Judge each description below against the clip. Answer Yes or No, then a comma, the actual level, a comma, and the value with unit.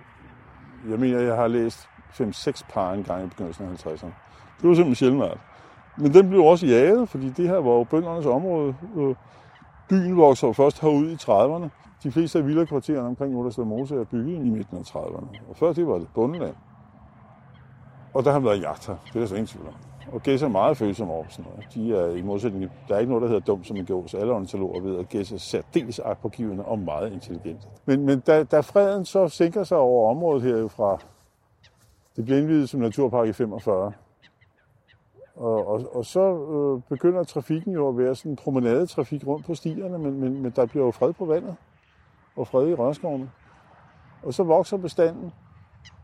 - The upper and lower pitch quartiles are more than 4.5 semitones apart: Yes, wide, 5.5 semitones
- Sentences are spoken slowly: No, average, 205 wpm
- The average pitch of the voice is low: Yes, low, 130 Hz